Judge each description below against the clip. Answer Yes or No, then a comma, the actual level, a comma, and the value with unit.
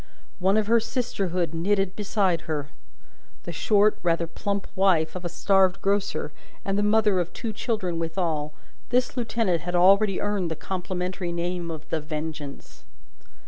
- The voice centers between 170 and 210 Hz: Yes, medium, 185 Hz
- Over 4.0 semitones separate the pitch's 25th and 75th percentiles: No, average, 3.6 semitones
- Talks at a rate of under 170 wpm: Yes, average, 150 wpm